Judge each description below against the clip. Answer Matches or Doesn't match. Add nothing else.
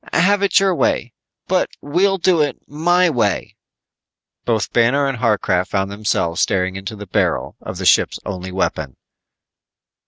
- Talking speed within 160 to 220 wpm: Doesn't match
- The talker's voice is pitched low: Matches